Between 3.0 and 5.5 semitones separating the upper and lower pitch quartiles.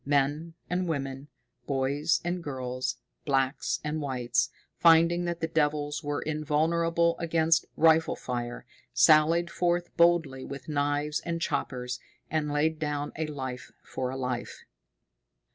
Yes: average, 3.5 semitones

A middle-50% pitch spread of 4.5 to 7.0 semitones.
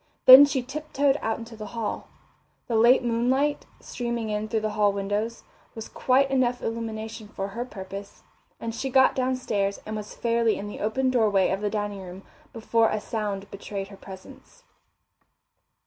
No: average, 3.2 semitones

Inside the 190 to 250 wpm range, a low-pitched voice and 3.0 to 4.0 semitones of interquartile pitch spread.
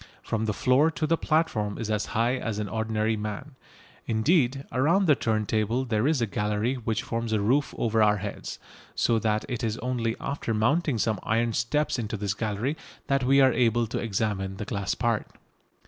Yes: average, 195 wpm; low, 115 Hz; average, 3.3 semitones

